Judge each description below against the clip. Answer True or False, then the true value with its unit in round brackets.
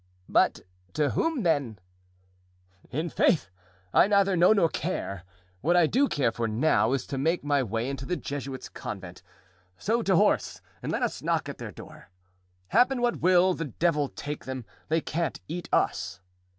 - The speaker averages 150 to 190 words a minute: True (165 wpm)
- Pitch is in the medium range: True (155 Hz)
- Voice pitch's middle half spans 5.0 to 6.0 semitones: True (5.5 semitones)